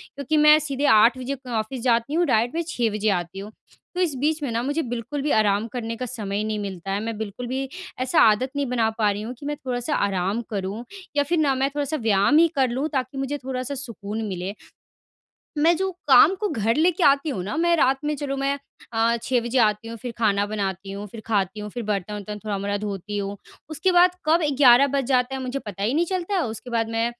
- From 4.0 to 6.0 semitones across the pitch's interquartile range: Yes, average, 5.0 semitones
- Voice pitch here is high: Yes, high, 240 Hz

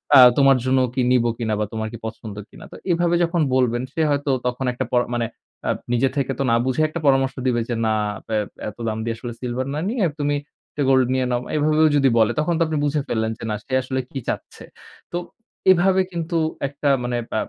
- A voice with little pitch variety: No, average, 4.0 semitones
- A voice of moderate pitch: No, low, 130 Hz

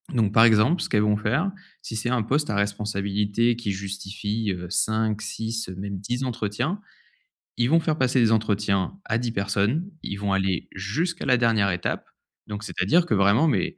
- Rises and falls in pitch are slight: No, average, 3.5 semitones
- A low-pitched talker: Yes, low, 110 Hz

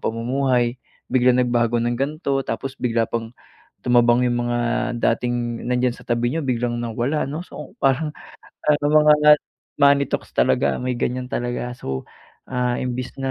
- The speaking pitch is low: Yes, low, 125 Hz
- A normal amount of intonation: No, narrow, 2.1 semitones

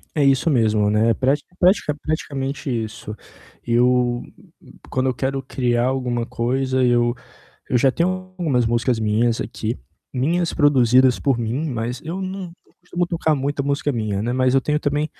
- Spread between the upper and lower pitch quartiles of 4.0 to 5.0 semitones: No, average, 3.5 semitones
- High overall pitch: No, low, 130 Hz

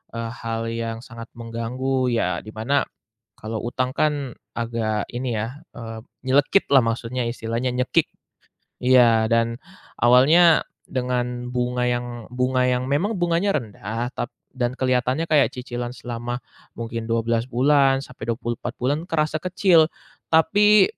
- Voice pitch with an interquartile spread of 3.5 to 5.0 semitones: No, narrow, 2.5 semitones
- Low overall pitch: Yes, low, 125 Hz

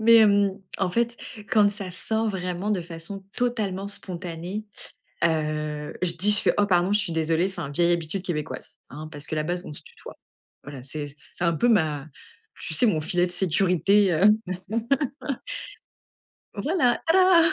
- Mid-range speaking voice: Yes, medium, 180 Hz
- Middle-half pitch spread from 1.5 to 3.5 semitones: No, average, 4.2 semitones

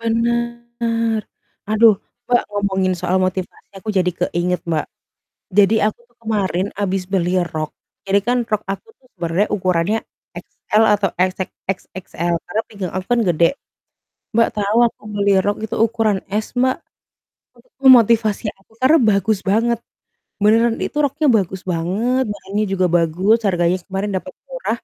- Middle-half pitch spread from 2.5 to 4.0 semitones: Yes, average, 3.6 semitones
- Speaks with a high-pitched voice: Yes, high, 205 Hz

